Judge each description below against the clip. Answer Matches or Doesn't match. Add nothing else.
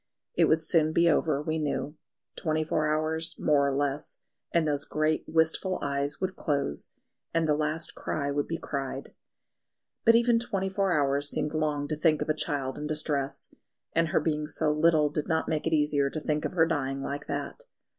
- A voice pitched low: Doesn't match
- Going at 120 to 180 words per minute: Doesn't match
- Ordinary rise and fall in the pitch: Doesn't match